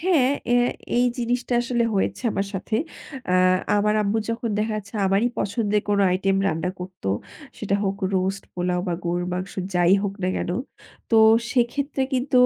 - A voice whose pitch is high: Yes, high, 205 Hz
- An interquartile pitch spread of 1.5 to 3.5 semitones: No, average, 4.3 semitones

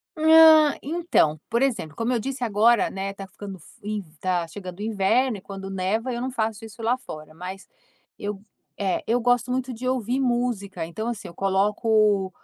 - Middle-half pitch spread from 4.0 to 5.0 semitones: Yes, average, 4.3 semitones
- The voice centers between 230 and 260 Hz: No, high, 215 Hz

